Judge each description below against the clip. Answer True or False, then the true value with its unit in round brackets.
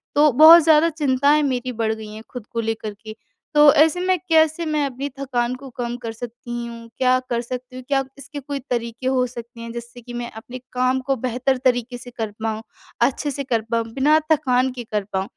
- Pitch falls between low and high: False (250 Hz)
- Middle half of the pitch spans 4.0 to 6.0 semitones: False (3.0 semitones)